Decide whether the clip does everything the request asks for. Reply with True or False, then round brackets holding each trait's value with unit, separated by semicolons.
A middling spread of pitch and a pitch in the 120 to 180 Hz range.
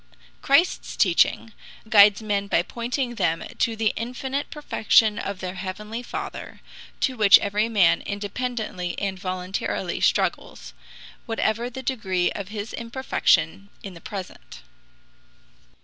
False (3.6 semitones; 210 Hz)